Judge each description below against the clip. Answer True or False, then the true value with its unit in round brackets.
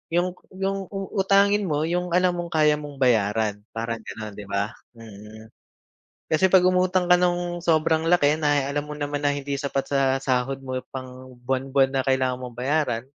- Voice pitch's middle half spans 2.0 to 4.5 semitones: False (5.6 semitones)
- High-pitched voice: False (145 Hz)